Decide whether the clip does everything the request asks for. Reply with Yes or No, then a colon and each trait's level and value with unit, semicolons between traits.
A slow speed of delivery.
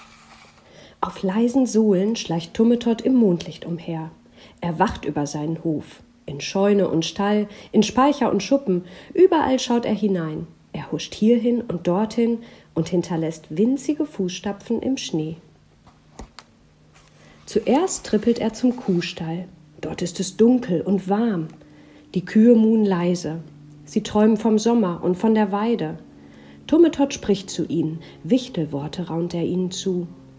No: average, 135 wpm